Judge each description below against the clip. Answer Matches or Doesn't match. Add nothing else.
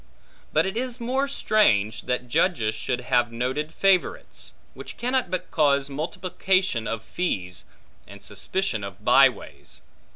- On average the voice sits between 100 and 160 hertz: Matches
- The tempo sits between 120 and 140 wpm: Matches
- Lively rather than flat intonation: Matches